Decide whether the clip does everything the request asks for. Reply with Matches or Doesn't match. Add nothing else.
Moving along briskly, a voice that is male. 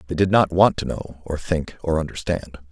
Matches